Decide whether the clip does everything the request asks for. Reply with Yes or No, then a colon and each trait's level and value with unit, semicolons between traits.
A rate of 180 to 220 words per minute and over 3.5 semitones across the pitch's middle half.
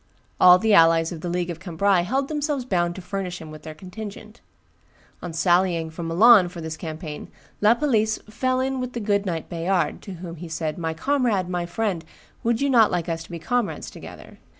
Yes: fast, 205 wpm; average, 4.9 semitones